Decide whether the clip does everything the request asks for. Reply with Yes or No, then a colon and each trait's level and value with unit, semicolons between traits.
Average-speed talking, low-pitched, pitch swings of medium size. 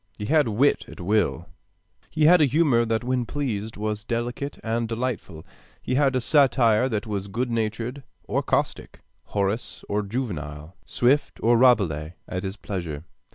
Yes: average, 155 wpm; low, 115 Hz; average, 3.9 semitones